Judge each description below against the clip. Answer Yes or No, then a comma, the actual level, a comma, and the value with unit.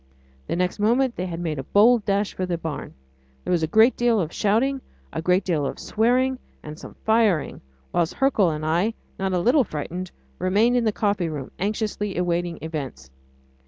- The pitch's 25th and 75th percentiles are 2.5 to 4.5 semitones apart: No, average, 5.0 semitones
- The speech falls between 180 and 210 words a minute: Yes, average, 190 wpm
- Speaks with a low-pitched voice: No, medium, 185 Hz